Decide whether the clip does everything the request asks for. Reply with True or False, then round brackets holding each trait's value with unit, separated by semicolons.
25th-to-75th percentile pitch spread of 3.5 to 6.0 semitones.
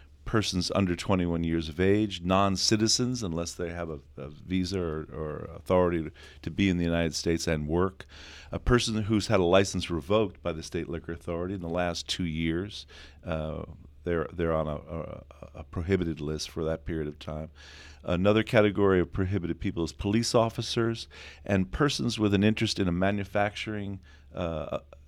True (3.8 semitones)